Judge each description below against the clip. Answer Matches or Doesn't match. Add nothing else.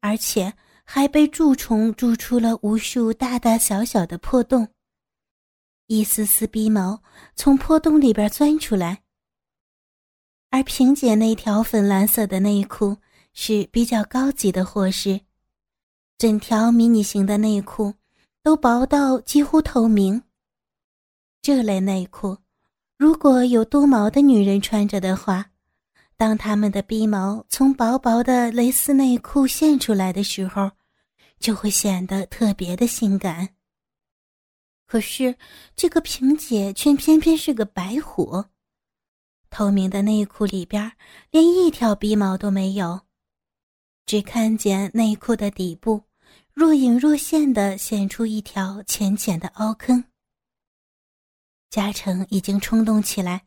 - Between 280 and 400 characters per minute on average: Doesn't match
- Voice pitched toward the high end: Matches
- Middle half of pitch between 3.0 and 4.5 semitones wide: Matches